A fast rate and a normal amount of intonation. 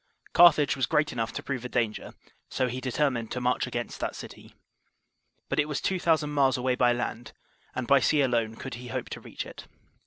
Yes: fast, 210 wpm; average, 3.1 semitones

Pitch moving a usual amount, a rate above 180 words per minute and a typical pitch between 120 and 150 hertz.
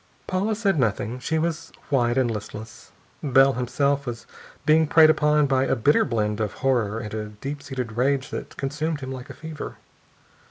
No: average, 4.3 semitones; average, 175 wpm; low, 135 Hz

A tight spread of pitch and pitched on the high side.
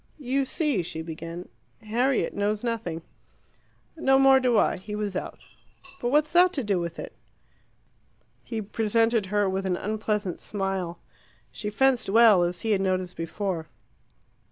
No: average, 4.6 semitones; high, 210 Hz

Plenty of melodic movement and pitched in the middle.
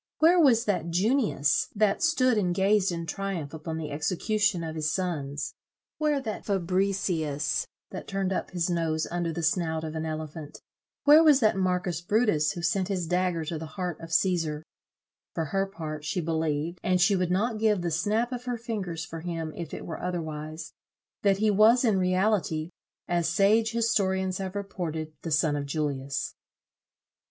No: average, 4.2 semitones; medium, 180 Hz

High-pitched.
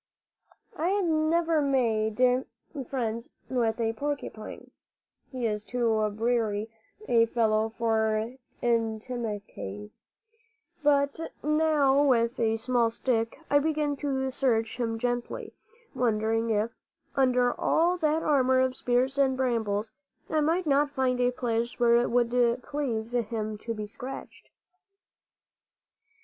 Yes: high, 245 Hz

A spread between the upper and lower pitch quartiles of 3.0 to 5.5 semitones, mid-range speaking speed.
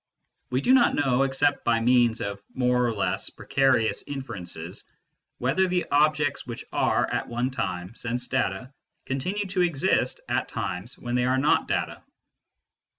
Yes: average, 3.4 semitones; average, 150 wpm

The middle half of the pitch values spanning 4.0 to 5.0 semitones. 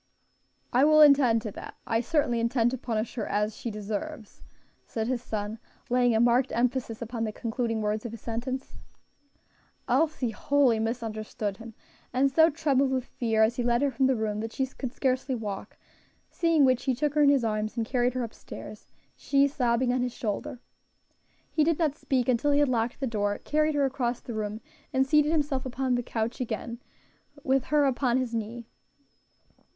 No: average, 3.1 semitones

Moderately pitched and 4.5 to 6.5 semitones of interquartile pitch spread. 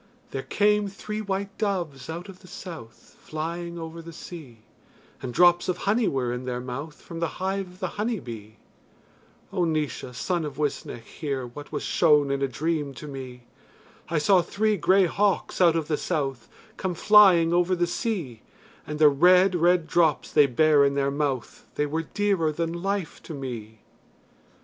Yes: medium, 165 Hz; average, 4.8 semitones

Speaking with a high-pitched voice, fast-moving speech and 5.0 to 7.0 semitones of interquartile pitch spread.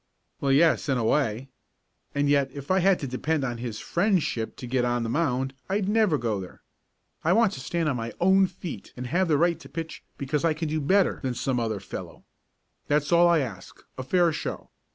No: medium, 145 Hz; fast, 215 wpm; wide, 5.5 semitones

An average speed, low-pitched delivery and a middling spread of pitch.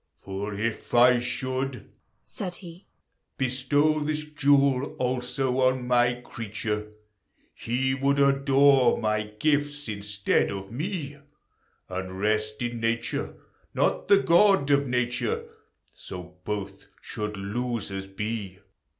No: slow, 110 wpm; low, 125 Hz; average, 4.7 semitones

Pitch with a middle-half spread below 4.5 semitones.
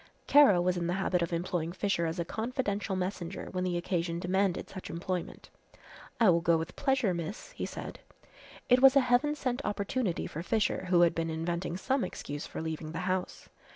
Yes: average, 4.1 semitones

